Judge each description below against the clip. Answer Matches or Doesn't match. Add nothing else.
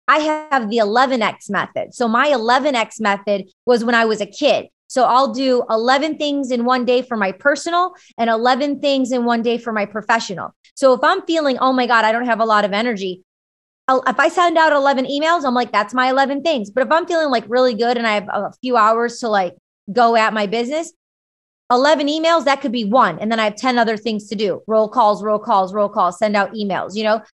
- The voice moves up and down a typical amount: Matches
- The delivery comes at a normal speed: Doesn't match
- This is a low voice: Doesn't match